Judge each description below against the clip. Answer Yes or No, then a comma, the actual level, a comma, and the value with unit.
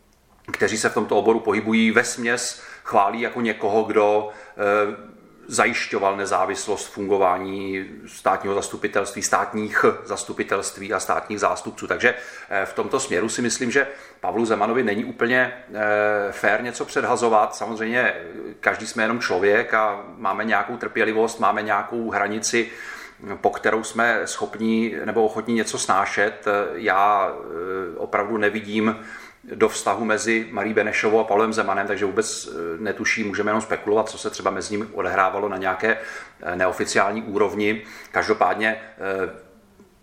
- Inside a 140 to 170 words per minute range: No, average, 125 wpm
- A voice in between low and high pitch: No, low, 110 Hz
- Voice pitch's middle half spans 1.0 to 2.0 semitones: Yes, narrow, 1.6 semitones